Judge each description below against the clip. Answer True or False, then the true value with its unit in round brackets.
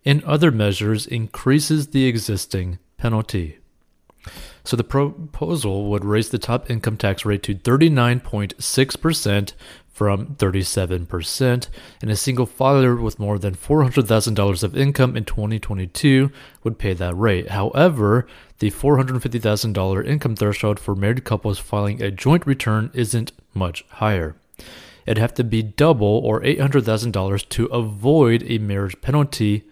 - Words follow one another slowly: True (130 wpm)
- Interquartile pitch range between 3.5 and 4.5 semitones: True (4.2 semitones)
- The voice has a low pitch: True (110 Hz)